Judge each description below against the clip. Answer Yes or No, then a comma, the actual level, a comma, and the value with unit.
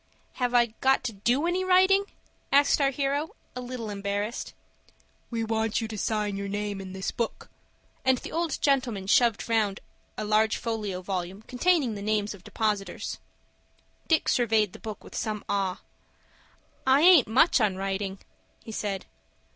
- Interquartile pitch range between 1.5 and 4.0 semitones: No, average, 4.4 semitones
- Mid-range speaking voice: No, high, 220 Hz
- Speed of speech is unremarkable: Yes, average, 160 wpm